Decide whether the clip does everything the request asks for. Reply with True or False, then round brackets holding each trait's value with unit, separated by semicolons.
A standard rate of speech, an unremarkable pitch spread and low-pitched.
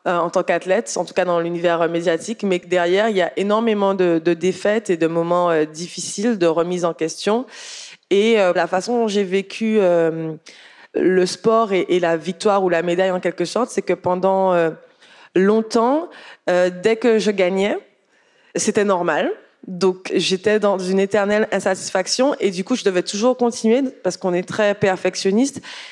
False (175 wpm; 3.8 semitones; 190 Hz)